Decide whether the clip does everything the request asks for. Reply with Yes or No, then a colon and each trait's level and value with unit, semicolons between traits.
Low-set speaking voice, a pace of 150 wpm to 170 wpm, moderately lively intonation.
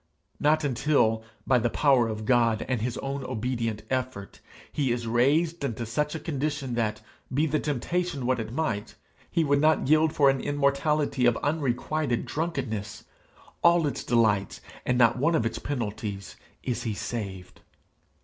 Yes: low, 130 Hz; average, 160 wpm; average, 4.5 semitones